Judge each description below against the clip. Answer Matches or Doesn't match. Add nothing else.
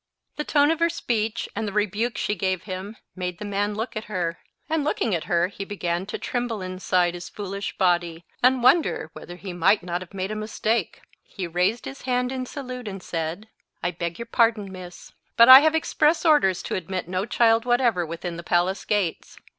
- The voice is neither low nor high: Doesn't match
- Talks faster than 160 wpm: Matches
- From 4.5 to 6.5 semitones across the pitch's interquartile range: Matches